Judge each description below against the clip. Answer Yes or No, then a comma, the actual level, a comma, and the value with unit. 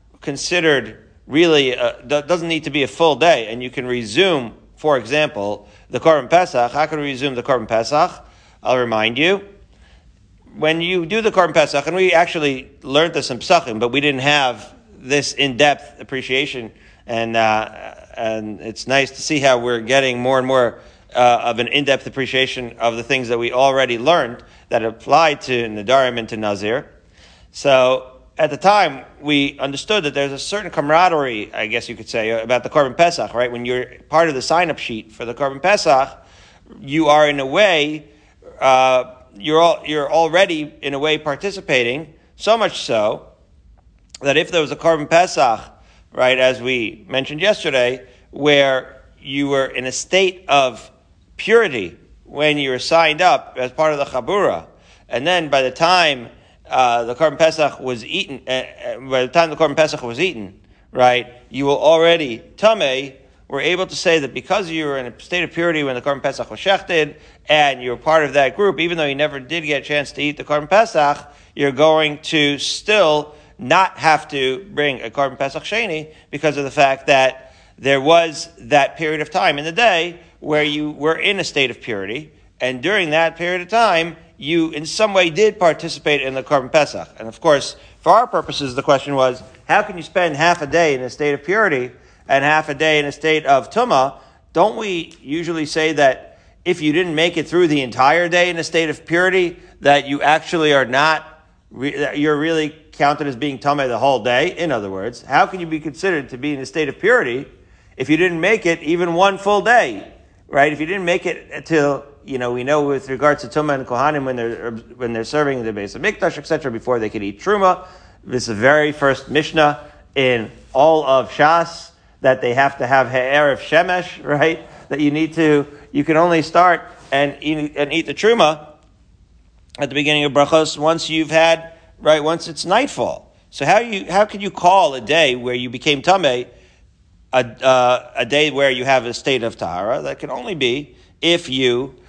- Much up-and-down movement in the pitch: No, average, 4.0 semitones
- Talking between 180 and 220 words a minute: Yes, average, 200 wpm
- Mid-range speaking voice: Yes, medium, 145 Hz